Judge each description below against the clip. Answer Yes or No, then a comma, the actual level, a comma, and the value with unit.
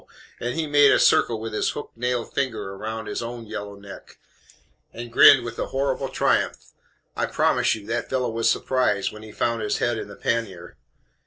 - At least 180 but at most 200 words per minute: Yes, average, 190 wpm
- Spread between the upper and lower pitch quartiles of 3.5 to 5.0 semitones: No, narrow, 2.6 semitones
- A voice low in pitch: Yes, low, 115 Hz